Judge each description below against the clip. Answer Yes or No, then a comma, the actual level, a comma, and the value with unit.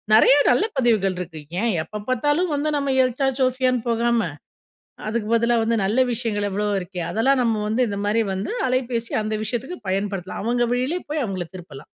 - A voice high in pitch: Yes, high, 230 Hz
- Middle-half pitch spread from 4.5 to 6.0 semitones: No, average, 3.7 semitones